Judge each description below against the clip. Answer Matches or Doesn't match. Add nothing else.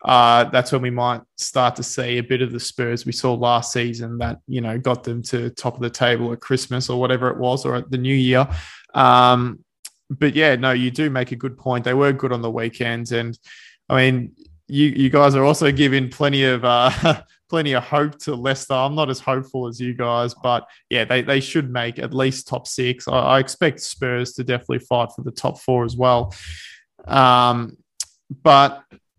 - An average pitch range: Doesn't match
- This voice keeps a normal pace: Doesn't match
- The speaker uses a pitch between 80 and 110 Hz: Doesn't match